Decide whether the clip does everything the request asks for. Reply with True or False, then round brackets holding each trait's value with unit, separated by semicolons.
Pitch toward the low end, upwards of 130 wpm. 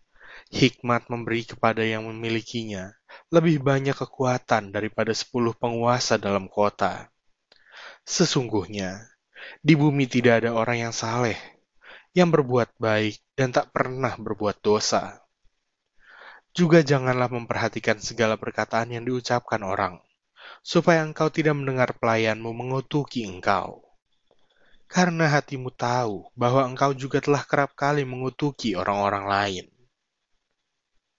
False (120 Hz; 110 wpm)